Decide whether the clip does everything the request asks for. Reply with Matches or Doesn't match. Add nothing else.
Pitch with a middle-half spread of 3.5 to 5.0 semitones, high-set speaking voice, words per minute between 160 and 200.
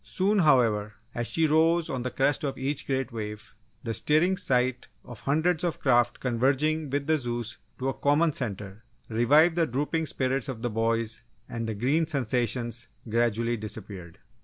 Doesn't match